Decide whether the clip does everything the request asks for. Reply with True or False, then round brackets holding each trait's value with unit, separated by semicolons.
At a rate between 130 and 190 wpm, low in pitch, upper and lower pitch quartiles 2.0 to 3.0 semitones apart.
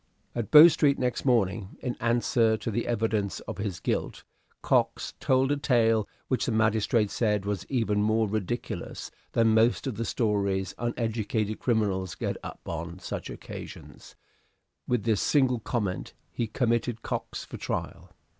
True (150 wpm; 110 Hz; 2.6 semitones)